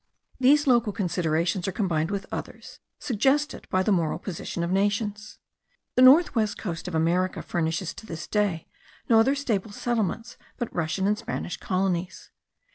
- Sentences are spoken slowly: No, average, 155 wpm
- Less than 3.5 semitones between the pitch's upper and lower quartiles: No, average, 4.5 semitones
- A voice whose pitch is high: Yes, high, 200 Hz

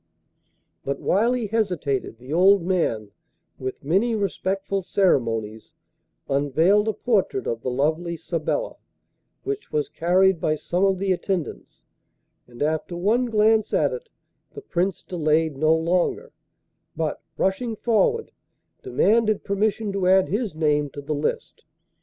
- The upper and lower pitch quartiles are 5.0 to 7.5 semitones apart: Yes, wide, 5.5 semitones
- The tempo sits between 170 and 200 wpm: No, slow, 135 wpm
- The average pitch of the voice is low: No, medium, 185 Hz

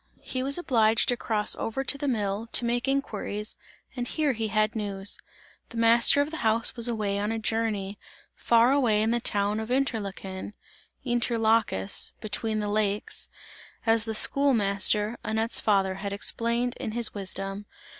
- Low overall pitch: No, high, 220 Hz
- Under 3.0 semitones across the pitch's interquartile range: Yes, narrow, 2.5 semitones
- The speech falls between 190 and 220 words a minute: No, average, 165 wpm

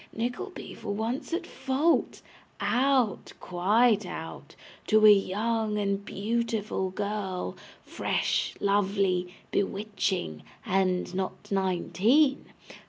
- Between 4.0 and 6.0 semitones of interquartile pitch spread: No, average, 3.4 semitones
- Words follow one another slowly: Yes, slow, 100 wpm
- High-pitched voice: Yes, high, 205 Hz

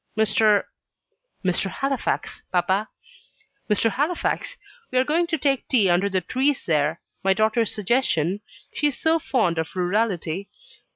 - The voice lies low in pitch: No, high, 215 Hz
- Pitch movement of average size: No, wide, 6.4 semitones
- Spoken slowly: Yes, slow, 130 wpm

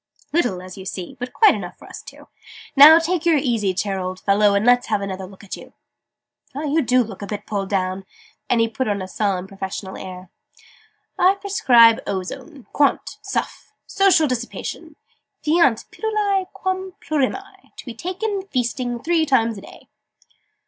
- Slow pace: No, average, 170 wpm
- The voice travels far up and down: Yes, wide, 8.8 semitones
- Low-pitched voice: No, high, 245 Hz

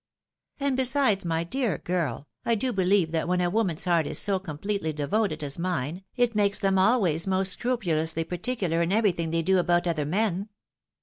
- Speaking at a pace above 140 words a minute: Yes, average, 190 wpm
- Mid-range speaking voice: Yes, medium, 180 Hz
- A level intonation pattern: No, average, 4.2 semitones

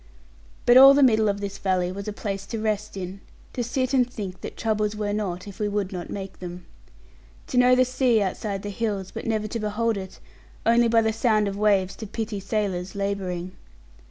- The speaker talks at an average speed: No, fast, 210 wpm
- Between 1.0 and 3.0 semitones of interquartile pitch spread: Yes, narrow, 2.6 semitones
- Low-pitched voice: No, high, 210 Hz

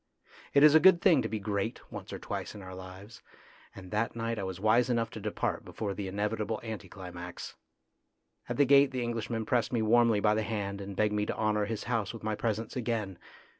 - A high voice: No, low, 110 Hz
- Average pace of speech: No, fast, 220 wpm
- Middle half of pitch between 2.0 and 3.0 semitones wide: Yes, narrow, 2.5 semitones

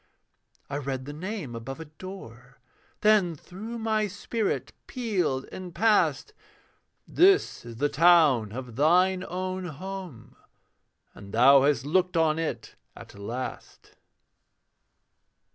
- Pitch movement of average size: No, wide, 6.2 semitones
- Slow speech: Yes, slow, 115 wpm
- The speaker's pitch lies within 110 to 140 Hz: No, medium, 165 Hz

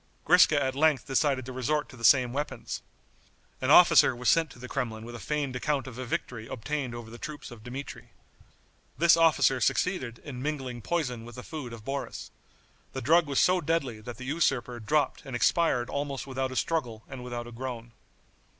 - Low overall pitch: Yes, low, 130 Hz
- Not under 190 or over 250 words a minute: Yes, average, 195 wpm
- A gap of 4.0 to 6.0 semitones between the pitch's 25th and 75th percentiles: No, average, 3.5 semitones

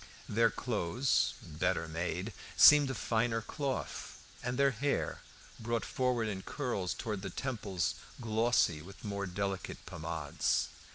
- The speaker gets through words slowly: Yes, slow, 125 wpm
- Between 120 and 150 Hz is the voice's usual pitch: No, low, 110 Hz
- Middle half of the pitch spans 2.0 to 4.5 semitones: No, average, 5.1 semitones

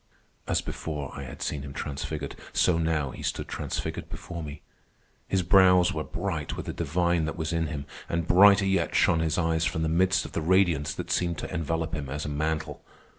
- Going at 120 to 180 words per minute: No, fast, 205 wpm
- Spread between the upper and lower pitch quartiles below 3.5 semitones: Yes, narrow, 2.5 semitones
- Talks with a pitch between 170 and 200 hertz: No, very low, 80 Hz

